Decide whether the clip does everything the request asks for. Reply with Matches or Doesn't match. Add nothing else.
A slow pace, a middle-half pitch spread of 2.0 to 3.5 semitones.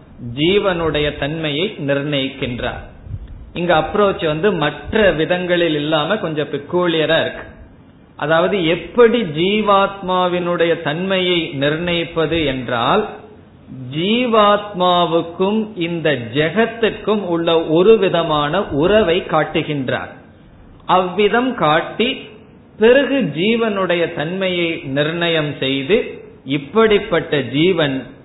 Doesn't match